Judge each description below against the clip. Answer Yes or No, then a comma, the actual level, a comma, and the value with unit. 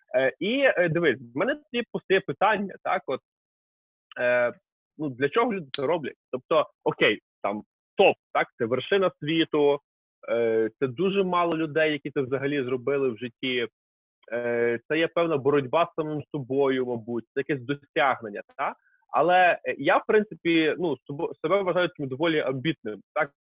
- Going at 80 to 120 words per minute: No, average, 145 wpm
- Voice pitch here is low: No, medium, 150 Hz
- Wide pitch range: Yes, wide, 5.7 semitones